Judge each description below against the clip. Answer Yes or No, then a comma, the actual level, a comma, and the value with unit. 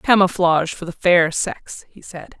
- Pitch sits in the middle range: Yes, medium, 175 Hz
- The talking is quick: No, average, 175 wpm